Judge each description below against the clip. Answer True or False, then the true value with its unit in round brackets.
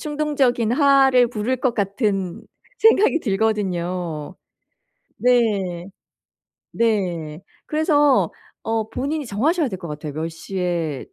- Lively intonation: True (7.0 semitones)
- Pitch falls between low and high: False (220 Hz)